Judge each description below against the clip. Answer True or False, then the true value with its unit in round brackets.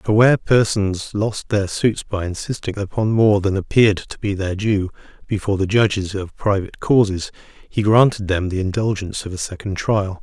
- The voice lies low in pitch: True (100 Hz)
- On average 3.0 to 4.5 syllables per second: False (5.2 syllables/s)